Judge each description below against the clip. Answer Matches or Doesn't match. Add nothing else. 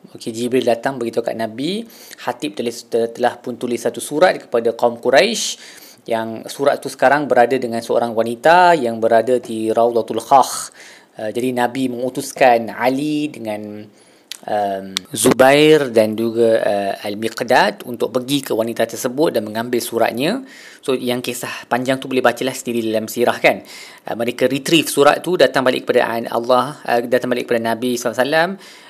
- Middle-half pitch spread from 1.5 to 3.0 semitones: Matches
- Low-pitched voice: Matches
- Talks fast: Matches